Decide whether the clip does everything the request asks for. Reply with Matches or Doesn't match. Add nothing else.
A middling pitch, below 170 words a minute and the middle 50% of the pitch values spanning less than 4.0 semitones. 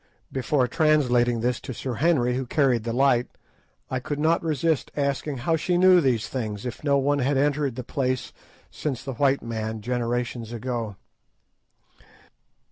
Doesn't match